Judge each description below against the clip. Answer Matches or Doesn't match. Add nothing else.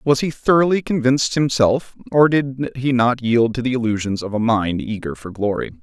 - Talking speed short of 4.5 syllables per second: Doesn't match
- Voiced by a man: Matches